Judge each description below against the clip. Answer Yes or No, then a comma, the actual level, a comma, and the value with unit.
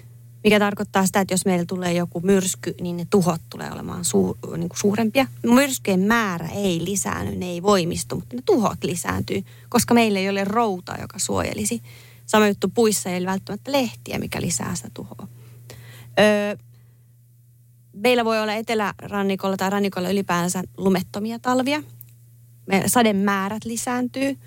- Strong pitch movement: Yes, wide, 9.0 semitones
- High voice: Yes, high, 195 Hz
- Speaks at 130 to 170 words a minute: Yes, average, 150 wpm